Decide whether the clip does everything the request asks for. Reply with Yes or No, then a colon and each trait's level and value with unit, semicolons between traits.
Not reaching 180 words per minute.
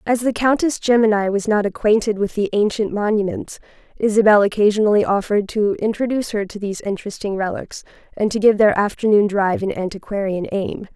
Yes: average, 165 wpm